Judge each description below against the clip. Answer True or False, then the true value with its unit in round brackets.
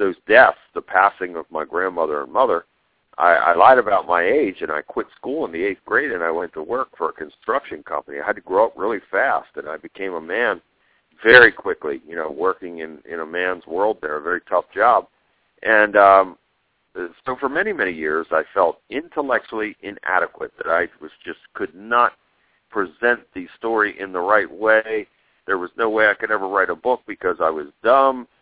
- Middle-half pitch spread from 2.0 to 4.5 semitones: False (5.5 semitones)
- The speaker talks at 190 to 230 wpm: True (205 wpm)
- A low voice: True (105 Hz)